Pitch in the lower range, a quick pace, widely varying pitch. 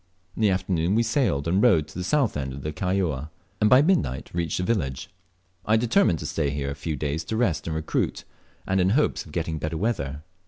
Yes: very low, 85 Hz; fast, 220 wpm; wide, 6.3 semitones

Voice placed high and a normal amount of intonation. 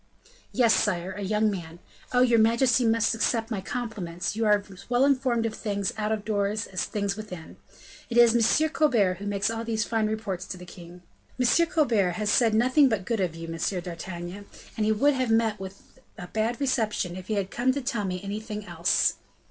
Yes: high, 215 Hz; average, 3.5 semitones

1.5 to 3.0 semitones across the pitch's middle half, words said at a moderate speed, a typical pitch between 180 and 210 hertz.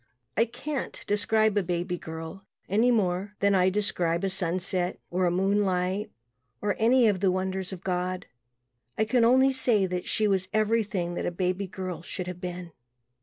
Yes: average, 2.7 semitones; average, 170 wpm; high, 190 Hz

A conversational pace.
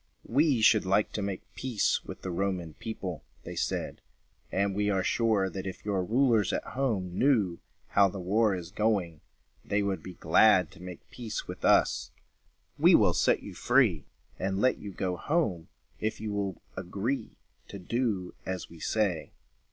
Yes: average, 170 wpm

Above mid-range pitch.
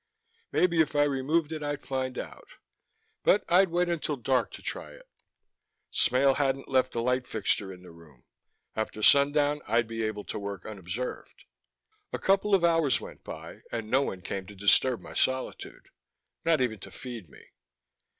No: low, 130 Hz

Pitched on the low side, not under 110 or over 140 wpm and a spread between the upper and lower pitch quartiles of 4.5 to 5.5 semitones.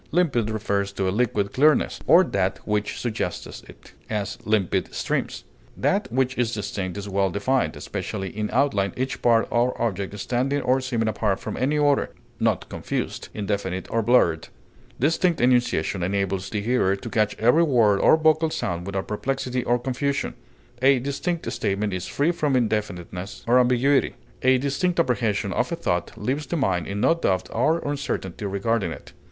No: low, 115 Hz; average, 165 wpm; average, 5.1 semitones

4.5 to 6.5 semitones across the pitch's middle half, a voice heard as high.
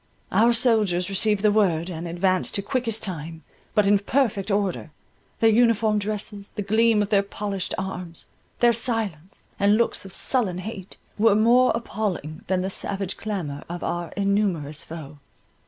No: average, 3.3 semitones; high, 200 Hz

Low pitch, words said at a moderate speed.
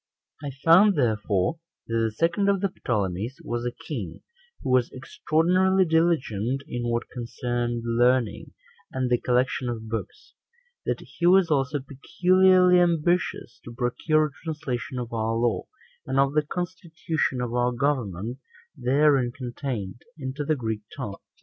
Yes: low, 130 Hz; average, 145 wpm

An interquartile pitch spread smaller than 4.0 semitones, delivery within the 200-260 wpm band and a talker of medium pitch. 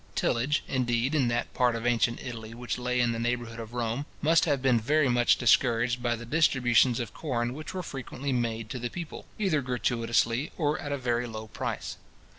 No: narrow, 2.6 semitones; fast, 205 wpm; low, 120 Hz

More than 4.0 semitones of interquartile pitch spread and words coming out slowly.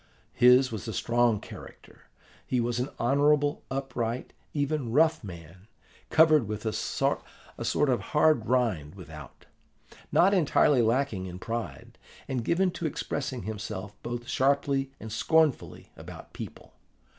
Yes: average, 4.6 semitones; slow, 130 wpm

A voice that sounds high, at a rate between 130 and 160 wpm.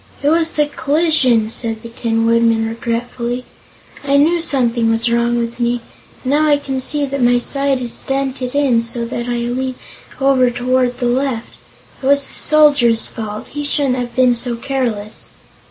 No: very high, 250 Hz; average, 175 wpm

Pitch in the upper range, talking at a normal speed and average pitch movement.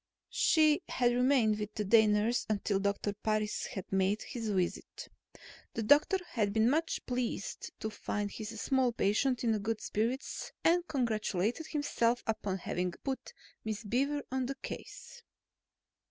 Yes: high, 225 Hz; average, 145 wpm; average, 3.9 semitones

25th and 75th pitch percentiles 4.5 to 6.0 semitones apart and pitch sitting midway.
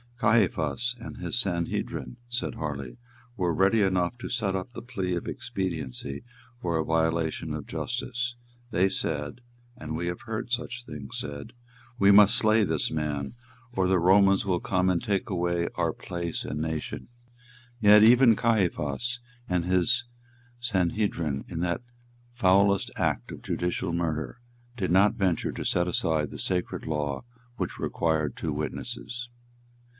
No: average, 5.2 semitones; very low, 90 Hz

